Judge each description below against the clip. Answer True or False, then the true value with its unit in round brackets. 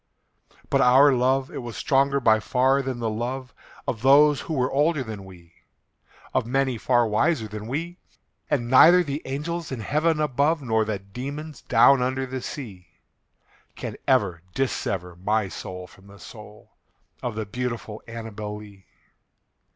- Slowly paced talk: False (155 wpm)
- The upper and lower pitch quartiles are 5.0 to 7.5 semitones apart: False (4.5 semitones)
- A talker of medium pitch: False (125 Hz)